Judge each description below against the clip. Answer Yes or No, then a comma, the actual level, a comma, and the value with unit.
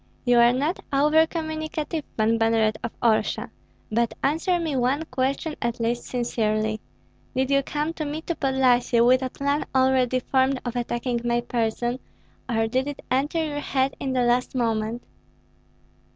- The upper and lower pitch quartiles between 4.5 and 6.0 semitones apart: No, average, 3.4 semitones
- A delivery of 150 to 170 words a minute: Yes, average, 160 wpm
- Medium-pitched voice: No, very high, 255 Hz